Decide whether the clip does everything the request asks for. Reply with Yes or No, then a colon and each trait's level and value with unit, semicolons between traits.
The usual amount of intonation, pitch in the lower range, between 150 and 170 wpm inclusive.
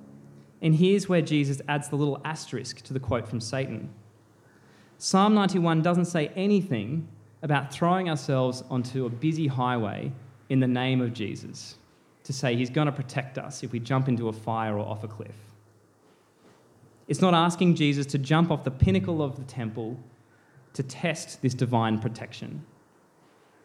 Yes: average, 5.0 semitones; low, 130 Hz; average, 160 wpm